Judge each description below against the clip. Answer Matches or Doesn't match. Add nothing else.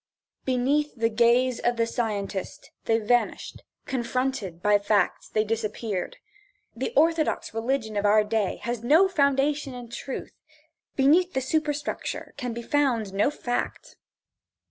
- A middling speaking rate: Doesn't match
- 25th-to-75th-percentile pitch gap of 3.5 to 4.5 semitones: Matches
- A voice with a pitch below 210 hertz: Doesn't match